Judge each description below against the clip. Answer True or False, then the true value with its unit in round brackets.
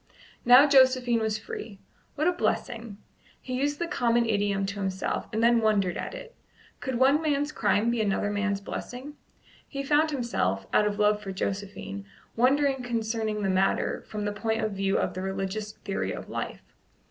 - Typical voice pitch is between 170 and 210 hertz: False (220 Hz)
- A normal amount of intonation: True (4.3 semitones)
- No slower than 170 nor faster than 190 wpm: True (175 wpm)